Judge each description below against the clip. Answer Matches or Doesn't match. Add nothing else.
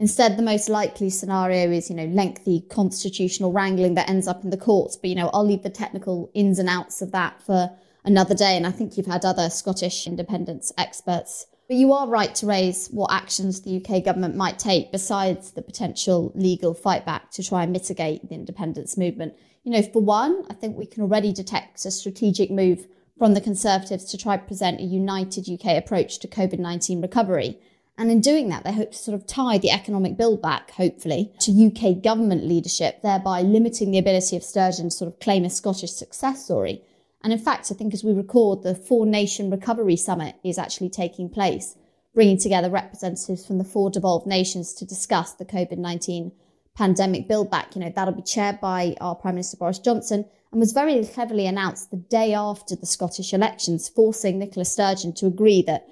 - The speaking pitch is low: Doesn't match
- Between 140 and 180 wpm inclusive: Doesn't match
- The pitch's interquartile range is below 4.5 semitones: Matches